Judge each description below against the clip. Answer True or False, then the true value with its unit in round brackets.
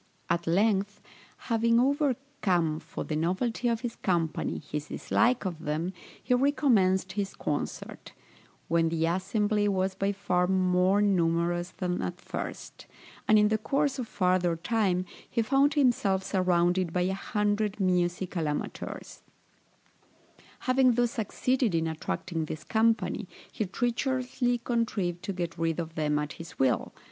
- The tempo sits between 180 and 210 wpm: False (140 wpm)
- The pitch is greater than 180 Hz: True (190 Hz)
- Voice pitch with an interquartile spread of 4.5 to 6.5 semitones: True (4.9 semitones)